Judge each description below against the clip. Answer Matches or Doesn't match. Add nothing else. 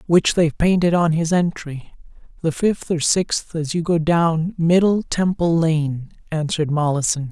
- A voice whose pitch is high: Doesn't match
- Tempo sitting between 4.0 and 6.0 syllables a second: Matches